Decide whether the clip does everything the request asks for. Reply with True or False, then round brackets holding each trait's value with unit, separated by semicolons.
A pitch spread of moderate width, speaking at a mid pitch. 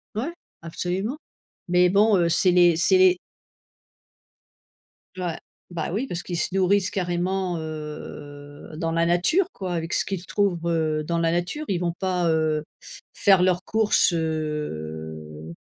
True (3.0 semitones; 175 Hz)